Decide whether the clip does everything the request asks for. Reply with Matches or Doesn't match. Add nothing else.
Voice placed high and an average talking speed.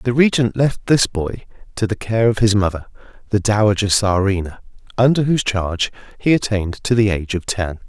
Doesn't match